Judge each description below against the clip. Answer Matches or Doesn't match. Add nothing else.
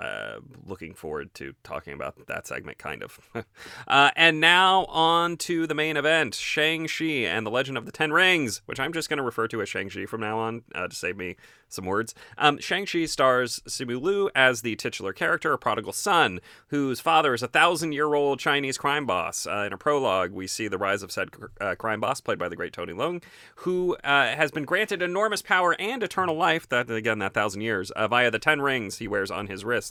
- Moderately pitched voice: Matches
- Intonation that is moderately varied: Doesn't match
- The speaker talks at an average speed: Doesn't match